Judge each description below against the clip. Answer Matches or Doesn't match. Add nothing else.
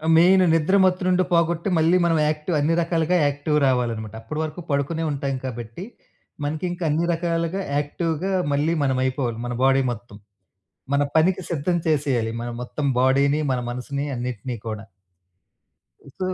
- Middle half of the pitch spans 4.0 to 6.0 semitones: Matches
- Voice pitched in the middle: Matches